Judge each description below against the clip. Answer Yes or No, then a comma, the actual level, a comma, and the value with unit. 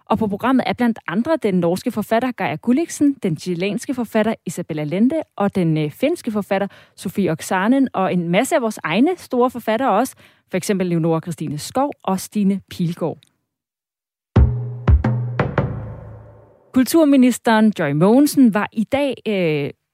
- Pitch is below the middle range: No, high, 205 Hz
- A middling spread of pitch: No, wide, 6.5 semitones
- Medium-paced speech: No, slow, 140 wpm